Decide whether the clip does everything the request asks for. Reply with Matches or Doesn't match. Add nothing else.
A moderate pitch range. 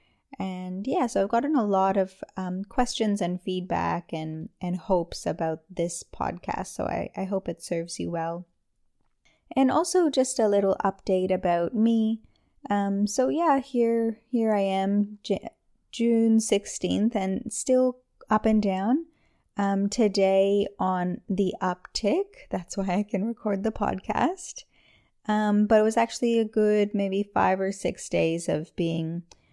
Matches